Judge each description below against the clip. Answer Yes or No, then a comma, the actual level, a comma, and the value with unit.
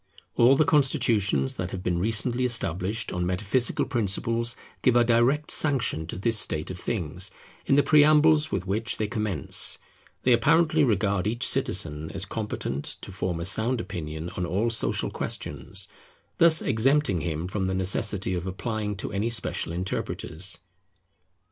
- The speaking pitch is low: Yes, low, 105 Hz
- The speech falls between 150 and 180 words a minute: Yes, average, 155 wpm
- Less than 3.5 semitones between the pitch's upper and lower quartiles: No, average, 4.9 semitones